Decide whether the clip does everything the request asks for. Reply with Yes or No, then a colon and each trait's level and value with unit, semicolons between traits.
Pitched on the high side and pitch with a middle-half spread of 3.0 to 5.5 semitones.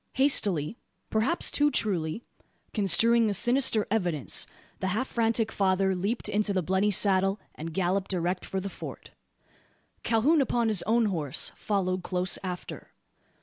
Yes: high, 200 Hz; average, 3.7 semitones